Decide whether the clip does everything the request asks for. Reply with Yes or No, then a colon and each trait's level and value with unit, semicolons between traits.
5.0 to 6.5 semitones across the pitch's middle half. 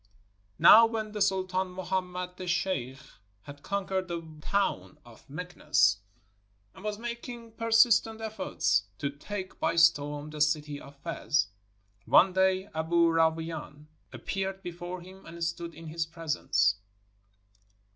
No: average, 3.8 semitones